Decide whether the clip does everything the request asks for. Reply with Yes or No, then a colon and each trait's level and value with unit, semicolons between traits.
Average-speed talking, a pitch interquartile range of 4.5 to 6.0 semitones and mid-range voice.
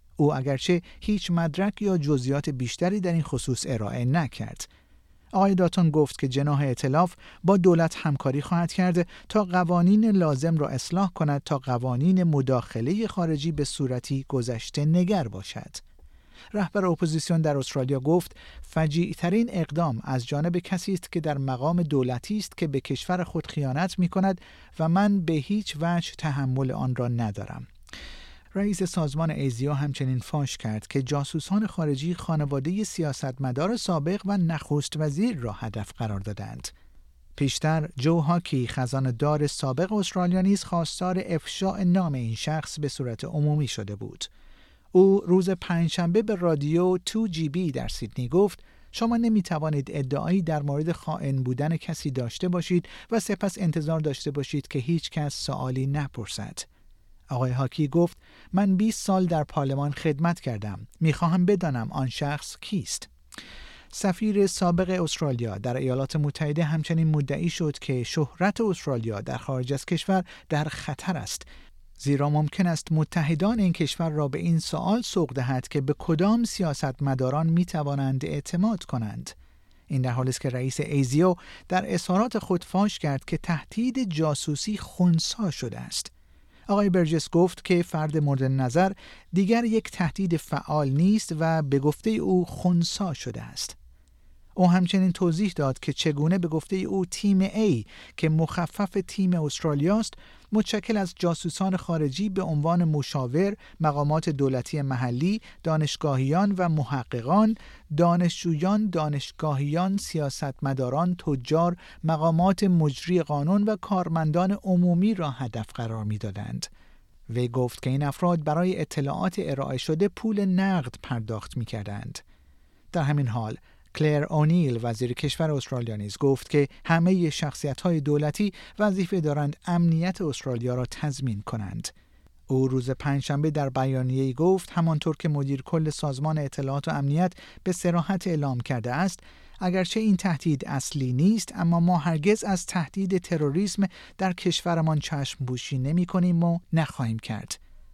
Yes: average, 140 wpm; average, 5.1 semitones; medium, 155 Hz